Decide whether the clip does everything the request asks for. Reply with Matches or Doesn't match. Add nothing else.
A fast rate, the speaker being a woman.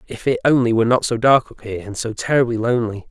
Doesn't match